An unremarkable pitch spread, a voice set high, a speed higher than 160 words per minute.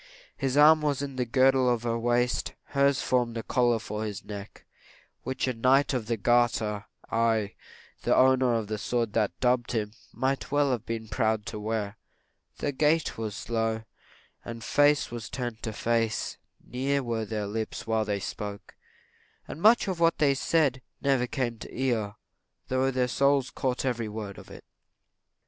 No: average, 3.1 semitones; low, 120 Hz; average, 175 wpm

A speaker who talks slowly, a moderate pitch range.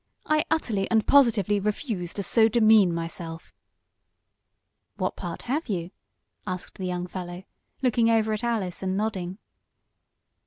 Yes: slow, 130 wpm; average, 4.0 semitones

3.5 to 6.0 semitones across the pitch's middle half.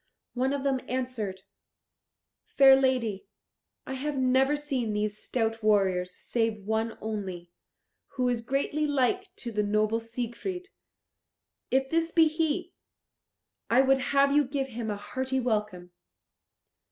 Yes: average, 4.1 semitones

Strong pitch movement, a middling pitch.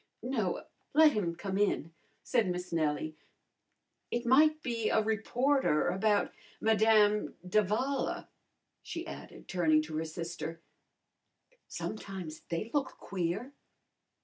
No: wide, 5.9 semitones; high, 205 Hz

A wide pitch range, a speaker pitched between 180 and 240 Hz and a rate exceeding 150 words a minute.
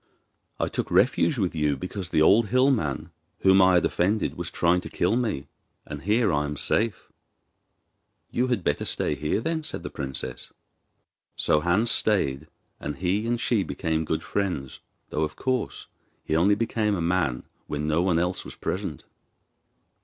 No: wide, 5.9 semitones; very low, 90 Hz; average, 170 wpm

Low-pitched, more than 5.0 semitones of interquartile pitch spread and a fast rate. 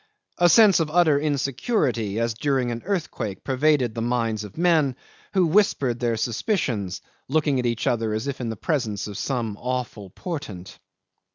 No: low, 125 Hz; wide, 5.4 semitones; average, 165 wpm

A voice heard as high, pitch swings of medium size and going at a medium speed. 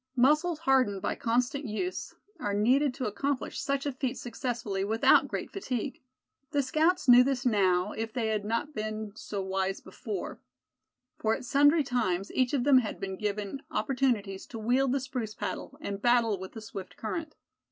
Yes: high, 240 Hz; average, 4.6 semitones; average, 175 wpm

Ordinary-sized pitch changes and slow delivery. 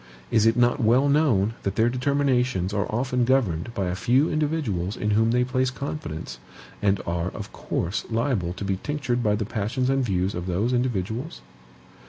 No: average, 4.9 semitones; average, 180 wpm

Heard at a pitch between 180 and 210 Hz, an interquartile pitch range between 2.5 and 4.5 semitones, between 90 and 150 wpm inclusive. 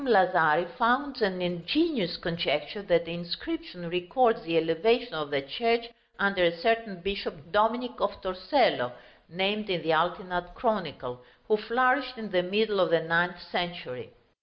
No: medium, 185 Hz; average, 5.0 semitones; average, 145 wpm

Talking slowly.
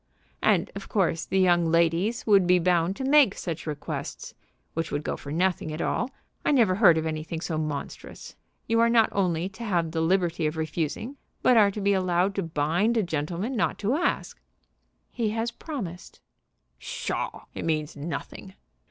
No: average, 180 wpm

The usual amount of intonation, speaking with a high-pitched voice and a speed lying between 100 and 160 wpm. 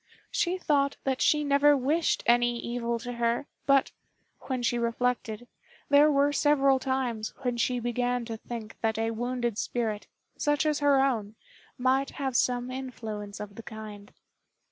Yes: average, 3.0 semitones; high, 245 Hz; average, 155 wpm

